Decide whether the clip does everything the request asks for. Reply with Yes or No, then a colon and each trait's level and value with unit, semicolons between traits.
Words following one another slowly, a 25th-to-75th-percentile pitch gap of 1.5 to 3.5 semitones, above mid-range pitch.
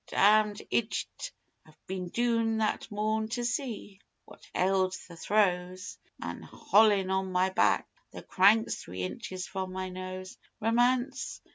Yes: slow, 130 wpm; average, 3.1 semitones; high, 200 Hz